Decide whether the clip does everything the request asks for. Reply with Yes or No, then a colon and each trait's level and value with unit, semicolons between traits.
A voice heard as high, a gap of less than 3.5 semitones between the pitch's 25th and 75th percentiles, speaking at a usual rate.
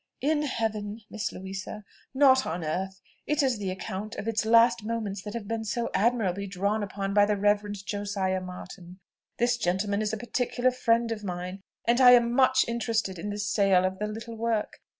Yes: high, 210 Hz; average, 3.1 semitones; average, 190 wpm